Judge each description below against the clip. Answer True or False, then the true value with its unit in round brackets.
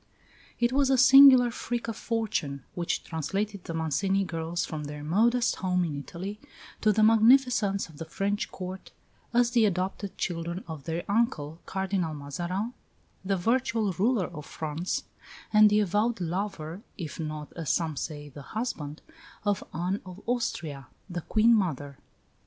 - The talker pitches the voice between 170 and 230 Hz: True (190 Hz)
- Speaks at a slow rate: False (150 wpm)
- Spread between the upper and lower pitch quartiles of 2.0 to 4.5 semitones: False (5.3 semitones)